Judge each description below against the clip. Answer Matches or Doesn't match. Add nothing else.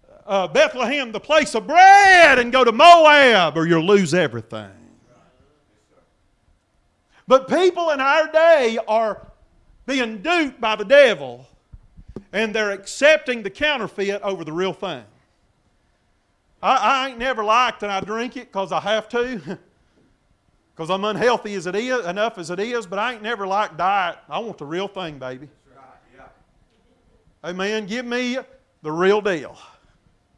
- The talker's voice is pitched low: Doesn't match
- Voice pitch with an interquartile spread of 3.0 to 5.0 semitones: Doesn't match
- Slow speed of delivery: Doesn't match